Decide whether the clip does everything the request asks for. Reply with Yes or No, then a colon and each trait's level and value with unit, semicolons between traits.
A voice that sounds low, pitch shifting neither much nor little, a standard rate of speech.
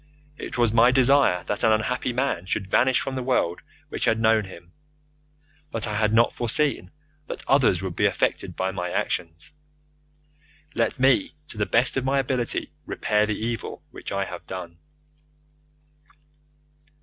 Yes: low, 110 Hz; average, 4.9 semitones; average, 160 wpm